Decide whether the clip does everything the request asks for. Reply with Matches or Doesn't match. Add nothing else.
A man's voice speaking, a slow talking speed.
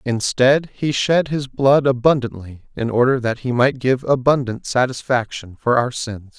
Doesn't match